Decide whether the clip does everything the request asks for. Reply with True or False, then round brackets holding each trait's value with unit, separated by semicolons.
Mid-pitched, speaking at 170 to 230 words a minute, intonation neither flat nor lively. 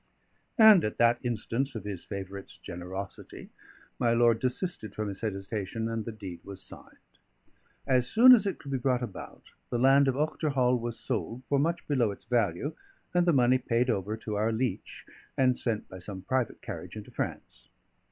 False (120 Hz; 180 wpm; 4.2 semitones)